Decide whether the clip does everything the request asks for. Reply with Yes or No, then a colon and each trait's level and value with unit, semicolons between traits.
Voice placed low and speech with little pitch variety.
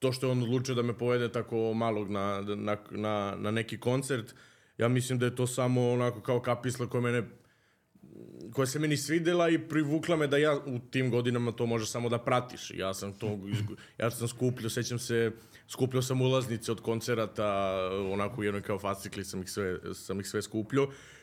No: low, 120 Hz; average, 3.3 semitones